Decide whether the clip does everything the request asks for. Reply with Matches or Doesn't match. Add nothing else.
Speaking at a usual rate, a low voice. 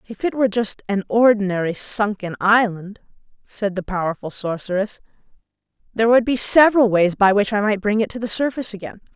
Doesn't match